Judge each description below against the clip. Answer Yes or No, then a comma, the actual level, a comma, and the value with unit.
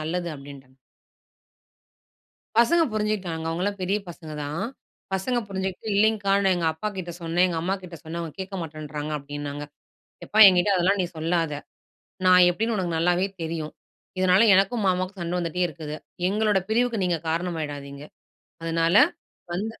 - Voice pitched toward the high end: No, medium, 175 Hz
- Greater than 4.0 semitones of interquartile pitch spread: No, average, 3.3 semitones